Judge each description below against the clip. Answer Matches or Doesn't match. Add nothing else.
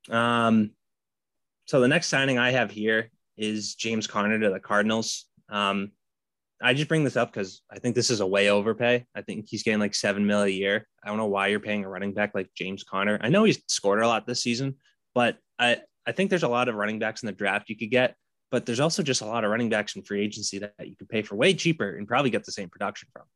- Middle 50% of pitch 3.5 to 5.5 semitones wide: Doesn't match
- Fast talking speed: Matches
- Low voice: Matches